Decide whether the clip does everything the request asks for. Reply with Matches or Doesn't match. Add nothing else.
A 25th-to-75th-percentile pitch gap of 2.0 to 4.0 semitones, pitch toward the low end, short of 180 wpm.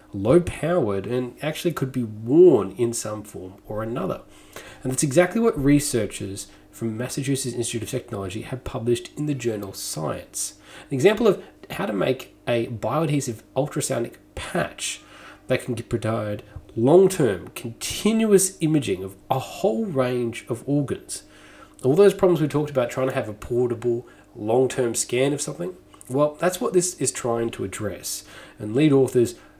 Doesn't match